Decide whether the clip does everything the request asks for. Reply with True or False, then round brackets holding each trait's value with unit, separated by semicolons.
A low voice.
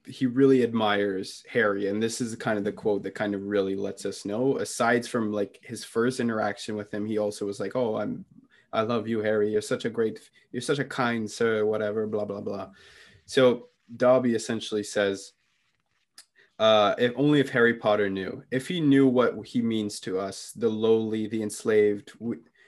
True (110 Hz)